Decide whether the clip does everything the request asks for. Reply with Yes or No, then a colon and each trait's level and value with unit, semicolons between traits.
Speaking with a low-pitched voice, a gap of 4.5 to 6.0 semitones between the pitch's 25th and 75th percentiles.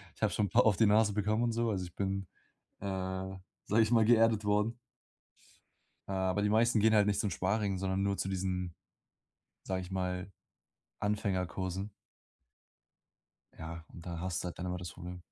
No: low, 100 Hz; average, 2.7 semitones